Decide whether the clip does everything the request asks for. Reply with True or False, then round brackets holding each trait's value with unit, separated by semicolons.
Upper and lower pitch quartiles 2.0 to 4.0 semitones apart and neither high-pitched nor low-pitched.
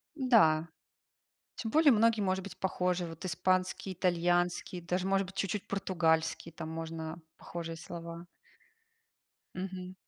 True (2.5 semitones; 180 Hz)